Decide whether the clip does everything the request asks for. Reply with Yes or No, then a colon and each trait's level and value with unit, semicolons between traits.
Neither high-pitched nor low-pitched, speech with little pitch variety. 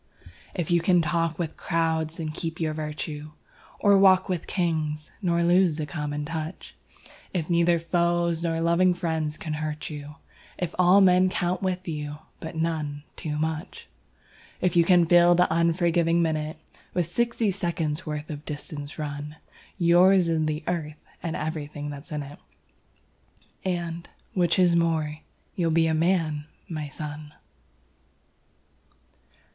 Yes: medium, 165 Hz; narrow, 2.2 semitones